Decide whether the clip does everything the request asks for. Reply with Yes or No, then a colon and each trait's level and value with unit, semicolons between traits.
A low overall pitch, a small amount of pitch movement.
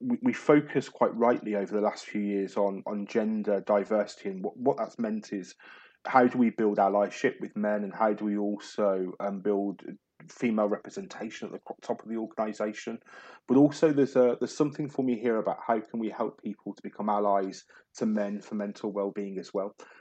No: low, 105 Hz; average, 3.5 semitones